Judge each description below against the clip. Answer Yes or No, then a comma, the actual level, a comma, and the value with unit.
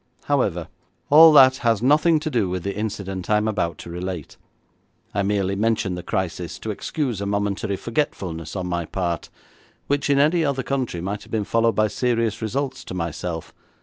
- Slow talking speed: No, average, 180 wpm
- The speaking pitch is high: No, low, 105 Hz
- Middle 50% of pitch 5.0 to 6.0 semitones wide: Yes, wide, 5.6 semitones